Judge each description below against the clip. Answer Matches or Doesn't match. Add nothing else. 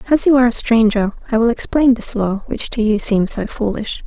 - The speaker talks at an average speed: Doesn't match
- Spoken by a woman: Matches